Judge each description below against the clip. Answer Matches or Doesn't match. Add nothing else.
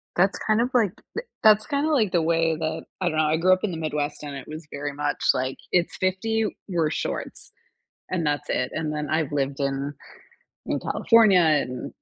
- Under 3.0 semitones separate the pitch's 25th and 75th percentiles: Doesn't match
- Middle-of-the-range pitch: Matches